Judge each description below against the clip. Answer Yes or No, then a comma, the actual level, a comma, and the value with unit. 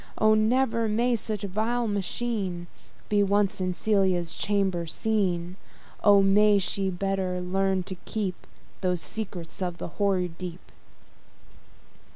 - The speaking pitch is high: Yes, high, 195 Hz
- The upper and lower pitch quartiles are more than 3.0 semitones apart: No, average, 2.7 semitones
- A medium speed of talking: No, slow, 130 wpm